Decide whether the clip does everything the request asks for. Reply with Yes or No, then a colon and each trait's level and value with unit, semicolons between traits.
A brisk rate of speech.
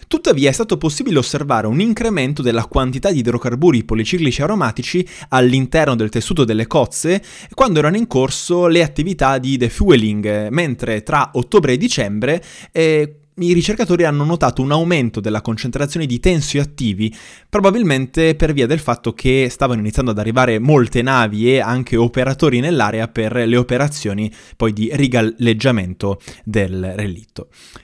No: average, 140 wpm